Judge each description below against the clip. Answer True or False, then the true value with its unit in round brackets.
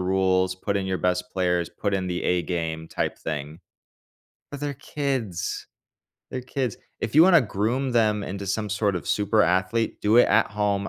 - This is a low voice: True (100 Hz)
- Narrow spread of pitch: False (3.8 semitones)